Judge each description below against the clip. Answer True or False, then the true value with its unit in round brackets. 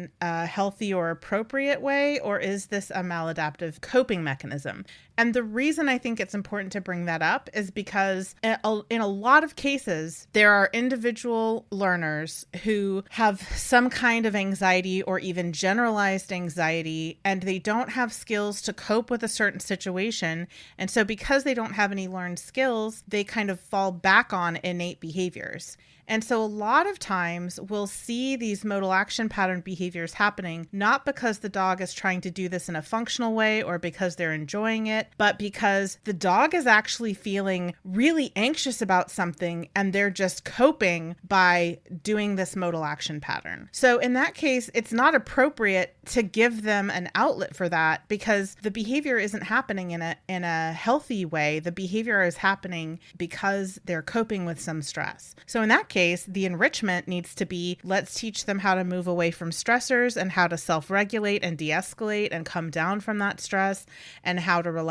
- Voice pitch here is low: False (195 Hz)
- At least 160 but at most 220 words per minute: True (180 wpm)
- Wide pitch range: False (3.9 semitones)